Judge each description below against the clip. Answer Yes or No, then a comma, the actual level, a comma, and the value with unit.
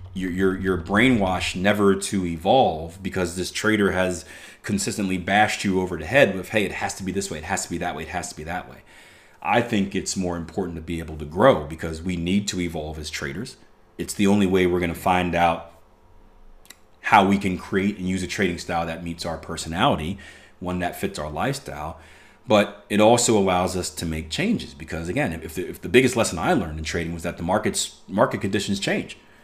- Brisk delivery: Yes, fast, 220 wpm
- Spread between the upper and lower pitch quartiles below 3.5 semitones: Yes, narrow, 2.5 semitones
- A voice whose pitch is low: Yes, very low, 90 Hz